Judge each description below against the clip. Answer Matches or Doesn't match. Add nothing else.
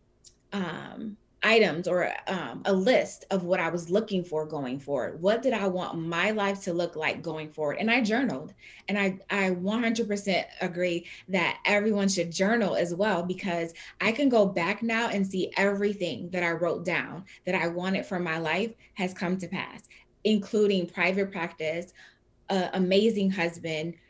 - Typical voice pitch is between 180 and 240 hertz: Matches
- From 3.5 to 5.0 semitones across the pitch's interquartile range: Doesn't match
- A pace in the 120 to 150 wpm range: Doesn't match